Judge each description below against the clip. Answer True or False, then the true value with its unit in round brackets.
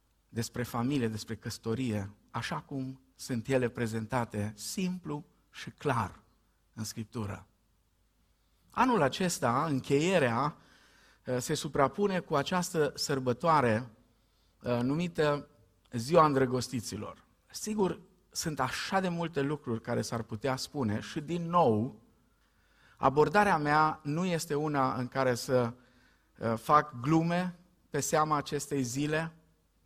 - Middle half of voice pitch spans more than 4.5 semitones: True (5.2 semitones)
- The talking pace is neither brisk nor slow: False (105 wpm)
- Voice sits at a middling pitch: False (130 Hz)